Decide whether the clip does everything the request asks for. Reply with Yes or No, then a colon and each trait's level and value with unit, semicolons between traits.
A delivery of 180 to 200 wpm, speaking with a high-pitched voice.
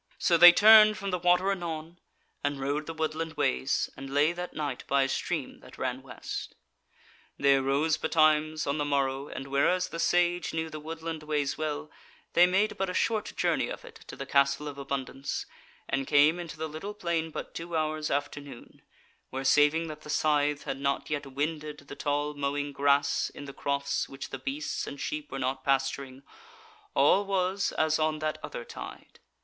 No: average, 190 wpm; medium, 150 Hz